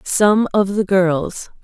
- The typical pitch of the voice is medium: No, high, 195 Hz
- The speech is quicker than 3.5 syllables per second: No, 2.9 syllables/s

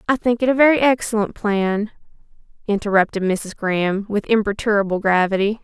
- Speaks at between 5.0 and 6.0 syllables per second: Yes, 5.6 syllables/s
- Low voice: No, high, 210 Hz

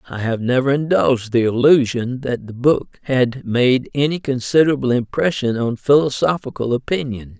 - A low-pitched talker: Yes, low, 130 Hz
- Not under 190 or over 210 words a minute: No, average, 140 wpm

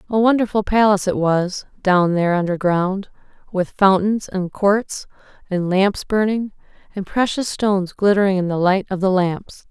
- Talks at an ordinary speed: Yes, average, 155 wpm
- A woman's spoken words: Yes, female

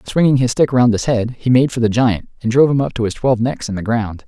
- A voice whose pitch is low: Yes, low, 120 Hz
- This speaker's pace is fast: Yes, fast, 325 wpm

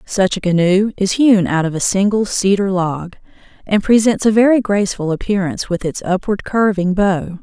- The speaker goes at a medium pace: Yes, average, 180 wpm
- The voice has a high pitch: Yes, high, 195 Hz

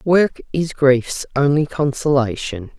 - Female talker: Yes, female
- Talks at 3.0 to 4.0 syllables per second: Yes, 3.7 syllables/s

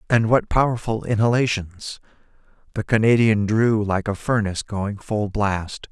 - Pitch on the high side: No, low, 105 Hz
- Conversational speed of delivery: No, slow, 130 wpm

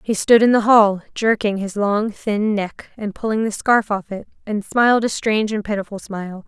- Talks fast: Yes, fast, 215 wpm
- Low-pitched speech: No, high, 210 Hz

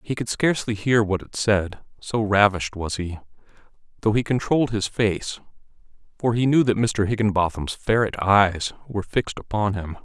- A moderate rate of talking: Yes, average, 165 wpm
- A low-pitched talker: Yes, low, 105 Hz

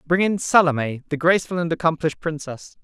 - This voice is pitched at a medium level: Yes, medium, 160 Hz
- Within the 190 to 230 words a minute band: No, average, 170 wpm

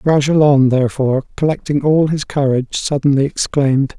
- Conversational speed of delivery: No, slow, 120 wpm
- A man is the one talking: Yes, male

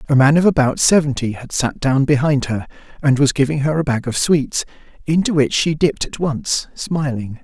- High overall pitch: No, medium, 140 Hz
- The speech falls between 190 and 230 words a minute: Yes, average, 200 wpm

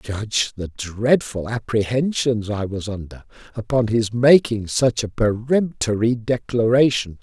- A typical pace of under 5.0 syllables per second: Yes, 4.8 syllables/s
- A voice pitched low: Yes, low, 115 Hz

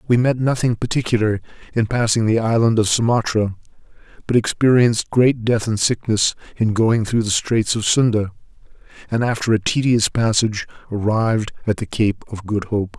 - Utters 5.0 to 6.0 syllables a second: Yes, 5.2 syllables/s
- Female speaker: No, male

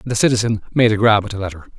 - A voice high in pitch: No, low, 105 Hz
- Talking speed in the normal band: No, fast, 270 wpm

